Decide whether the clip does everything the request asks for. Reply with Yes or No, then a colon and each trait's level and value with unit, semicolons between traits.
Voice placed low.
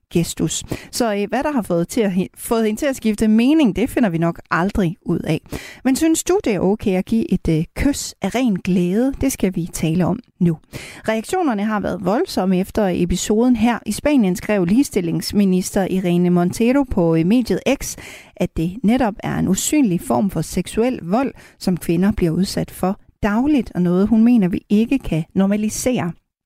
No: high, 205 Hz